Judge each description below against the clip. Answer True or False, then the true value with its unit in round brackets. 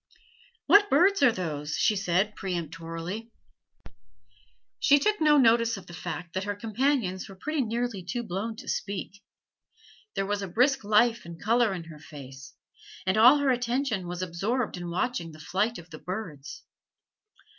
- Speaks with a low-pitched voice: False (205 Hz)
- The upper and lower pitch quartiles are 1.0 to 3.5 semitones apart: False (5.6 semitones)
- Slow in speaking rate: False (160 wpm)